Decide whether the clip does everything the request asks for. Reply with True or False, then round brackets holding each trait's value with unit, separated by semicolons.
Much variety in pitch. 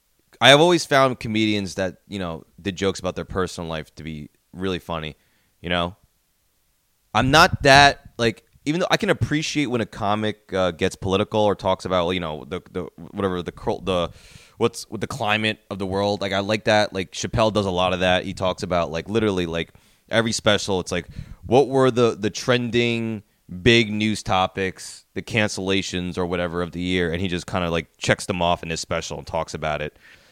False (3.8 semitones)